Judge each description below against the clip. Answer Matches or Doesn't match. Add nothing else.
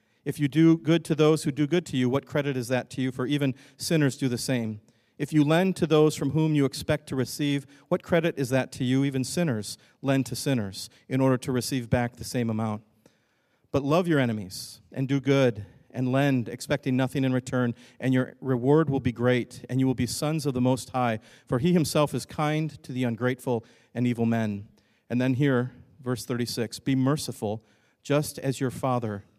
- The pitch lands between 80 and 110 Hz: Doesn't match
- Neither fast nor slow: Doesn't match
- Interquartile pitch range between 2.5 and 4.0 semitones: Matches